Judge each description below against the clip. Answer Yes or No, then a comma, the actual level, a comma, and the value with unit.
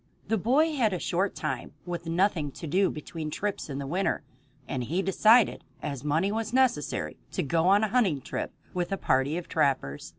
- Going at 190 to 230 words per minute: Yes, average, 195 wpm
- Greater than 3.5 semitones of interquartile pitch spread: Yes, wide, 5.6 semitones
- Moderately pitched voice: Yes, medium, 175 Hz